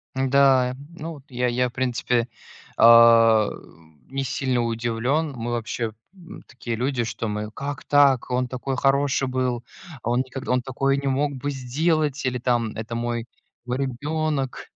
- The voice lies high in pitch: No, low, 130 Hz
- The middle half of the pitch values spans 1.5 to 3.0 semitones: Yes, narrow, 2.5 semitones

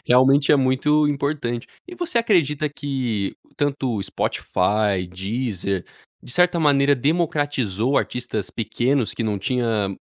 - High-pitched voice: No, low, 130 Hz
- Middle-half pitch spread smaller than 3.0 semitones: No, average, 5.0 semitones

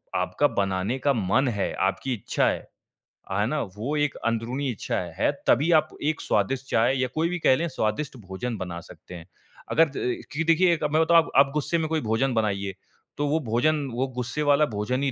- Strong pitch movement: Yes, wide, 5.9 semitones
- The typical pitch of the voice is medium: No, low, 130 Hz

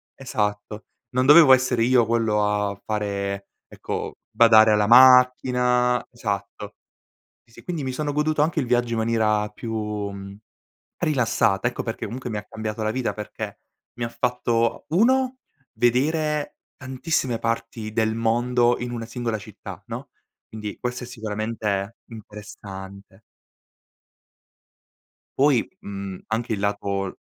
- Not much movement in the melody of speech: No, average, 3.1 semitones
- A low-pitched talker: Yes, low, 115 Hz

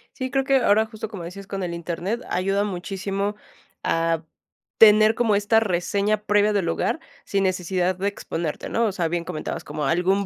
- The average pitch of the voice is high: Yes, high, 195 Hz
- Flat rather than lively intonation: No, average, 3.2 semitones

